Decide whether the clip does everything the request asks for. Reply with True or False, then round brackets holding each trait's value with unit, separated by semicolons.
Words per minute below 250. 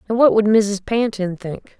True (200 wpm)